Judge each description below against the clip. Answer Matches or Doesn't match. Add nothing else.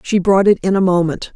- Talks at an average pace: Doesn't match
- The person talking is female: Matches